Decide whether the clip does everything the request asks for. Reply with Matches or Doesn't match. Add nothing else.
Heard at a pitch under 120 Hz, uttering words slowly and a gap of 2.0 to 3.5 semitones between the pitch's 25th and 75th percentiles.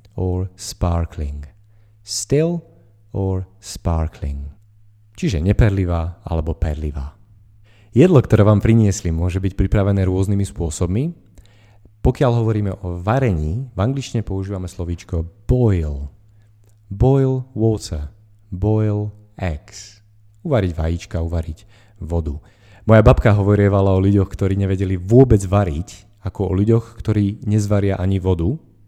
Matches